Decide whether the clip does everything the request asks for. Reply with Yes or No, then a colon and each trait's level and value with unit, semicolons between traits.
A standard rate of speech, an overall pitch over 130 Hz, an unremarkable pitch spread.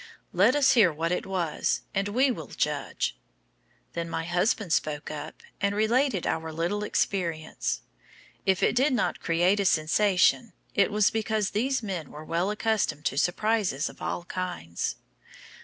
Yes: average, 155 wpm; high, 190 Hz; average, 4.5 semitones